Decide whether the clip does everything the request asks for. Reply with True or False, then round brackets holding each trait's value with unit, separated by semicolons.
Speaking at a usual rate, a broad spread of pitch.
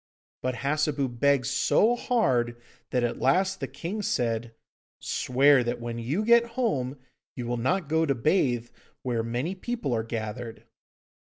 True (150 wpm; 6.0 semitones)